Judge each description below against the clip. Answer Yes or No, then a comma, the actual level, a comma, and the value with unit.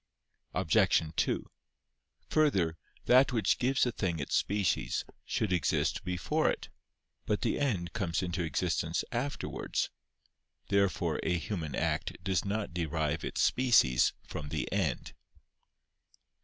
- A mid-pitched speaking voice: No, very low, 95 Hz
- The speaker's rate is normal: No, slow, 120 wpm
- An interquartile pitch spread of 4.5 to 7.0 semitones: Yes, wide, 5.4 semitones